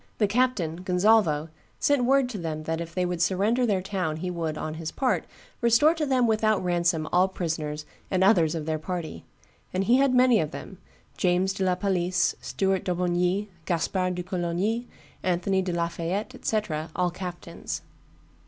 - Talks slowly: No, average, 170 wpm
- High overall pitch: No, medium, 180 Hz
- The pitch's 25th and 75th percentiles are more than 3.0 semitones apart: Yes, average, 3.9 semitones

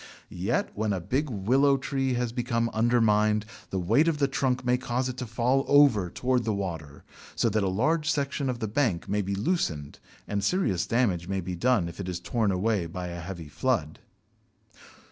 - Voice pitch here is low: Yes, low, 115 Hz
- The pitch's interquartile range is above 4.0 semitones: Yes, average, 5.3 semitones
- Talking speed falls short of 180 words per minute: No, average, 195 wpm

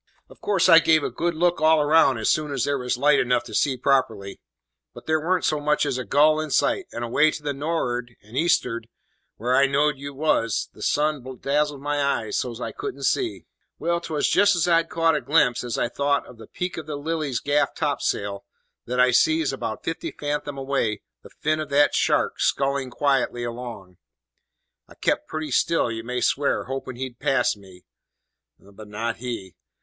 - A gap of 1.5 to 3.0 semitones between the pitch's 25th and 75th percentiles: No, average, 4.2 semitones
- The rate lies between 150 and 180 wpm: No, average, 195 wpm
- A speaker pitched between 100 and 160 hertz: Yes, medium, 140 Hz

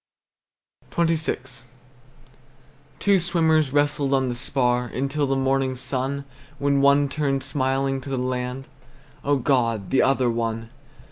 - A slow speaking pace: Yes, slow, 125 wpm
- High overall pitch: No, low, 135 Hz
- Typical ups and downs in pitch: No, narrow, 1.9 semitones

